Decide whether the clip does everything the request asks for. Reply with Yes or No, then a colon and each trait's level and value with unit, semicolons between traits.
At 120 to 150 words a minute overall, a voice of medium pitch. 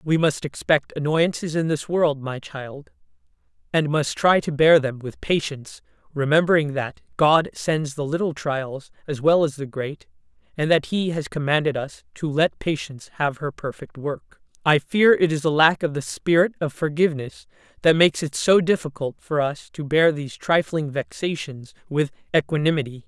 No: average, 175 wpm; medium, 150 Hz